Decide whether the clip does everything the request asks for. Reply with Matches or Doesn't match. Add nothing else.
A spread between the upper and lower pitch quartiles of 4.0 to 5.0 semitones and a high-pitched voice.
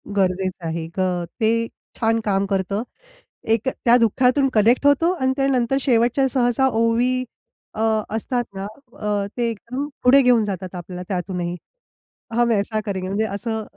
Matches